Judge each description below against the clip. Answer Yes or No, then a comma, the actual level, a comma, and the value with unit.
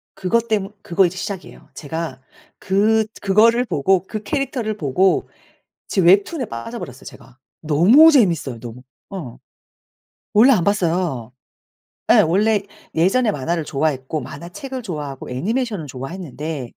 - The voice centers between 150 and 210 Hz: Yes, medium, 185 Hz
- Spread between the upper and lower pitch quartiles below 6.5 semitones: No, wide, 6.8 semitones